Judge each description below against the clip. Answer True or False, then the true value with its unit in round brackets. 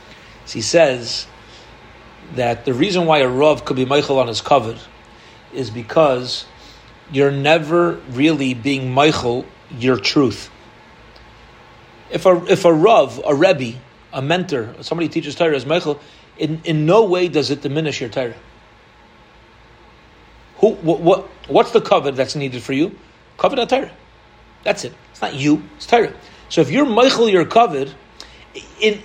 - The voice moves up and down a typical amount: True (4.0 semitones)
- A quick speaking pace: False (155 wpm)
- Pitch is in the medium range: True (145 Hz)